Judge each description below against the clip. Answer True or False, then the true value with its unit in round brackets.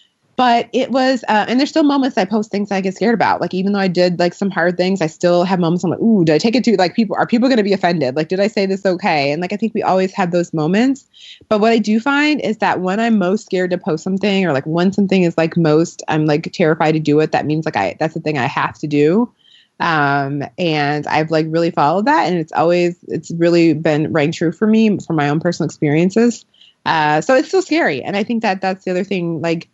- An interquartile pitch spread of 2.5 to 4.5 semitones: False (5.0 semitones)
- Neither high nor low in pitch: True (180 Hz)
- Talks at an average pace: False (270 wpm)